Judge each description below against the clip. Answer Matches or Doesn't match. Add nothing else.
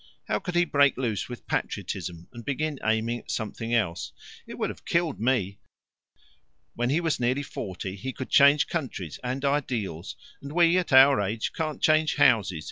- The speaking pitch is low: Matches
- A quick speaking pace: Doesn't match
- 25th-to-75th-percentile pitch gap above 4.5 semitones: Matches